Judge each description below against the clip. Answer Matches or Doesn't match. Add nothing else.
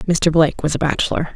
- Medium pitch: Matches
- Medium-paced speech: Doesn't match